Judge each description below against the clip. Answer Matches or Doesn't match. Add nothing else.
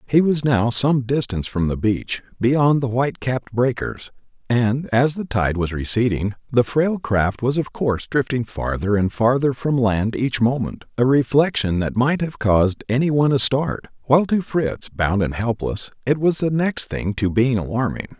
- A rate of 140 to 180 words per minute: Doesn't match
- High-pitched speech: Doesn't match